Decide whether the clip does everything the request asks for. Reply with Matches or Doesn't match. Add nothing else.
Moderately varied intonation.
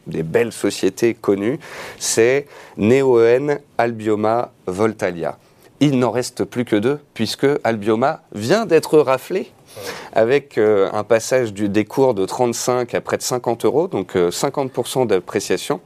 Matches